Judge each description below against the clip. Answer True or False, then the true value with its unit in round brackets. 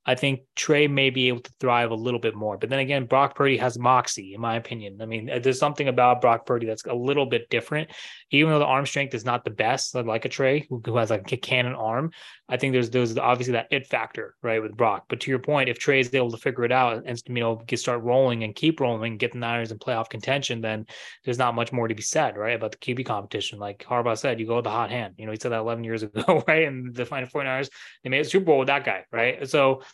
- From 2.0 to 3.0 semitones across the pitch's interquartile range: True (2.7 semitones)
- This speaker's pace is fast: True (275 wpm)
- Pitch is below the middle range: True (125 Hz)